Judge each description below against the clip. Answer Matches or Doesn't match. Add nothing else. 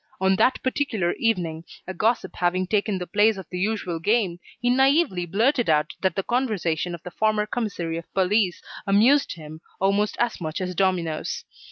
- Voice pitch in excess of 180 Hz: Matches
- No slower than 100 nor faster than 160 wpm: Doesn't match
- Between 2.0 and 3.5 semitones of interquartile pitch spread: Doesn't match